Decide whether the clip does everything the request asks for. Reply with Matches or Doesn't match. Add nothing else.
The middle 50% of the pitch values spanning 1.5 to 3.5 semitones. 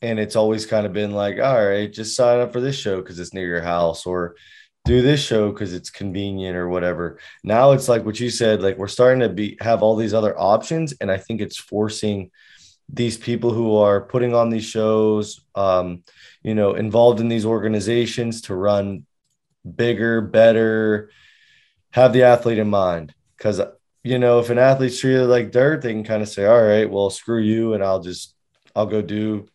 Matches